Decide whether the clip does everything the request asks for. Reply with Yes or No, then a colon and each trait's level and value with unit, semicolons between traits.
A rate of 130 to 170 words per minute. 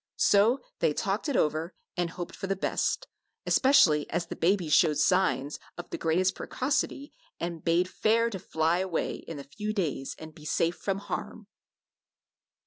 Yes: average, 165 wpm